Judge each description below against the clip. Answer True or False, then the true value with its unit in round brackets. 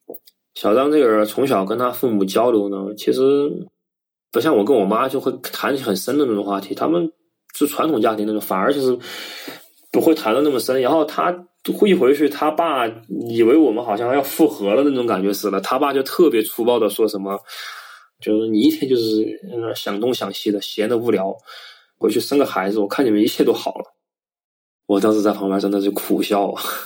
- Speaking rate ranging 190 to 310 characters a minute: True (295 characters per minute)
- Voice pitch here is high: False (115 Hz)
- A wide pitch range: True (5.8 semitones)